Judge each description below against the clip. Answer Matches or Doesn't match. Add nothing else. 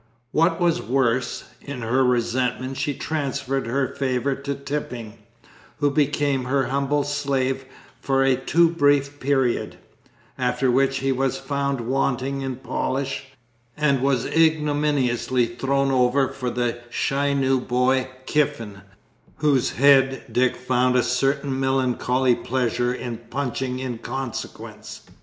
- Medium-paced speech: Doesn't match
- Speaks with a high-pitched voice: Doesn't match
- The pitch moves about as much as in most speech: Doesn't match